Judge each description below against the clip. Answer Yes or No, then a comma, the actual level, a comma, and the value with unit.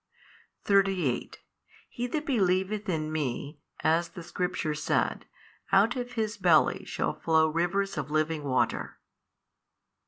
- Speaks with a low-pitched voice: No, medium, 175 Hz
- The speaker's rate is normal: No, slow, 120 wpm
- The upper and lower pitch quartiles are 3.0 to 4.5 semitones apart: Yes, average, 4.2 semitones